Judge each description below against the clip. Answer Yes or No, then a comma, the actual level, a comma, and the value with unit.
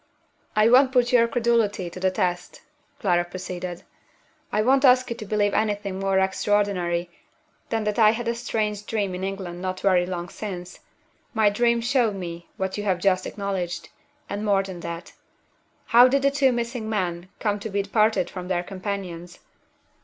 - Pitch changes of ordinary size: Yes, average, 3.5 semitones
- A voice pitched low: No, high, 200 Hz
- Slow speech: No, average, 175 wpm